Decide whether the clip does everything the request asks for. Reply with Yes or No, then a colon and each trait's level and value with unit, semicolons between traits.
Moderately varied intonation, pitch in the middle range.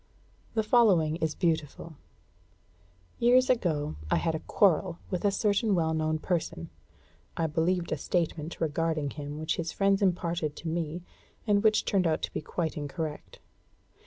Yes: average, 3.5 semitones; medium, 165 Hz